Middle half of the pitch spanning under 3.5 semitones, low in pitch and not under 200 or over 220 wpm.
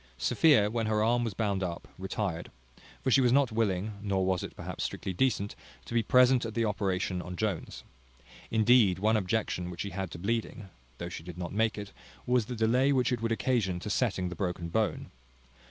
No: average, 3.8 semitones; low, 105 Hz; fast, 205 wpm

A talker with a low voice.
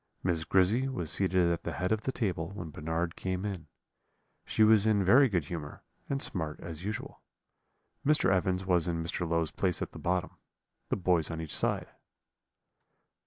Yes: very low, 90 Hz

